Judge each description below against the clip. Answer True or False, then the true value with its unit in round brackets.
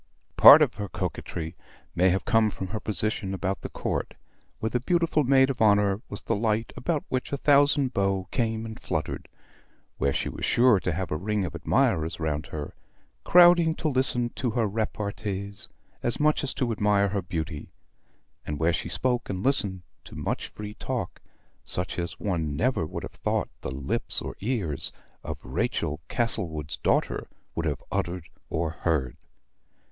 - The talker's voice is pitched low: True (100 Hz)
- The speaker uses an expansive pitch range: True (5.9 semitones)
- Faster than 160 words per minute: True (170 wpm)